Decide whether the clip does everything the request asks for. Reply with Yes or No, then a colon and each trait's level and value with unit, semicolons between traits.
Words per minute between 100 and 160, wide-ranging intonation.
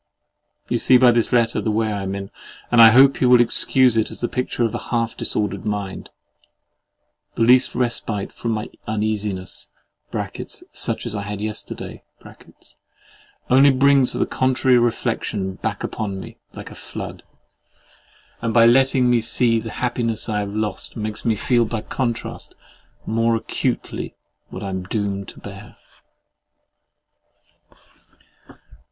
No: average, 145 wpm; average, 2.8 semitones